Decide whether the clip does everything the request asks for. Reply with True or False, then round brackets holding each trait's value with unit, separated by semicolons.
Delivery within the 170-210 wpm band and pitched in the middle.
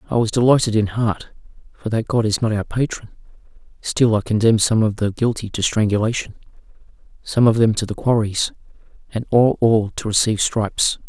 False (175 wpm; 110 Hz)